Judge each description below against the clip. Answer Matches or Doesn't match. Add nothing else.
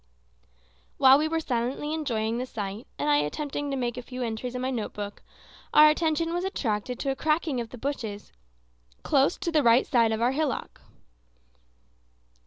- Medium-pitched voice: Doesn't match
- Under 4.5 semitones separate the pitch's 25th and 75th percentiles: Doesn't match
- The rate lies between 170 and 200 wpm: Matches